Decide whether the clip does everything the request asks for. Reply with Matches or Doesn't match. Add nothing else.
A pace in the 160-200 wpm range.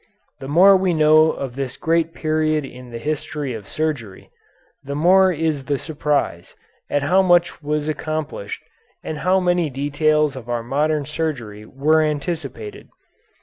Doesn't match